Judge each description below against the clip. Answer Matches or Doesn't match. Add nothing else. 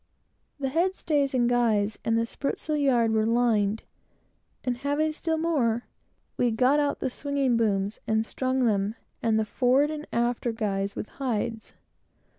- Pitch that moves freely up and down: Doesn't match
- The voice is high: Matches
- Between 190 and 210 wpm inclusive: Doesn't match